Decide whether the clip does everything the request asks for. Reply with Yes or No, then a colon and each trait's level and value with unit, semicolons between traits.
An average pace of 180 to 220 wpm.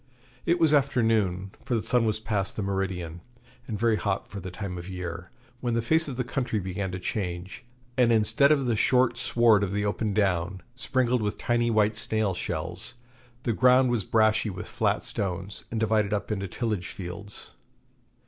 Yes: average, 185 wpm